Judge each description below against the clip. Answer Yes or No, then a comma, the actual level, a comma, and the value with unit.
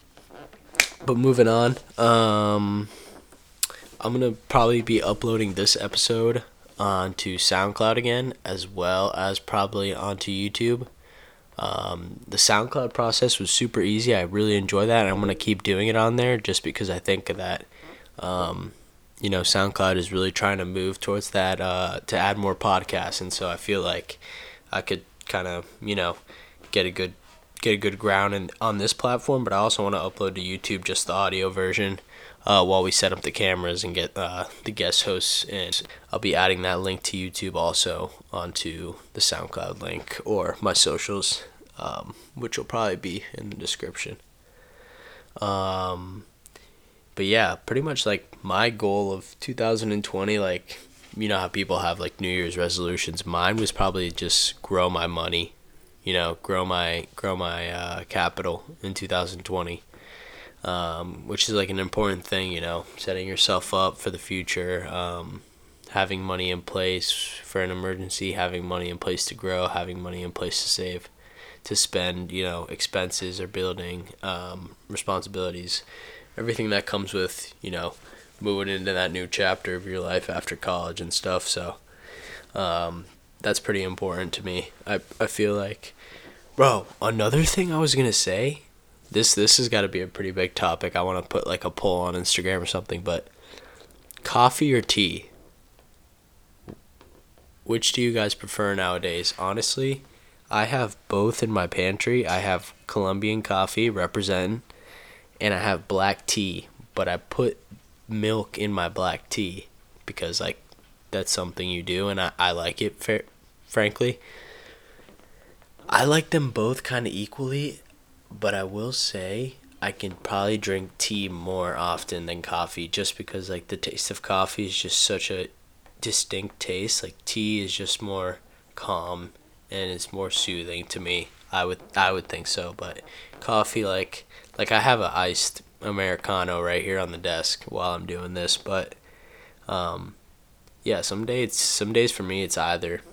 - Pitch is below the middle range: Yes, very low, 95 Hz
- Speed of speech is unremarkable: Yes, average, 170 wpm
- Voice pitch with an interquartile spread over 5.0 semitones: No, average, 2.9 semitones